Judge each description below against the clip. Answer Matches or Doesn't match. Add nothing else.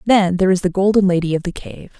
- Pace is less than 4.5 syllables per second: Doesn't match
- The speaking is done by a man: Doesn't match